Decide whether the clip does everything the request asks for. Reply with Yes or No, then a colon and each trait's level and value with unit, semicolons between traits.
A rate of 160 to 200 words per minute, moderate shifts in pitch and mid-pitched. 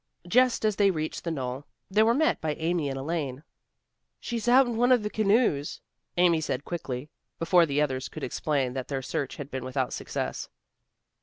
No: average, 185 wpm; wide, 7.6 semitones; medium, 160 Hz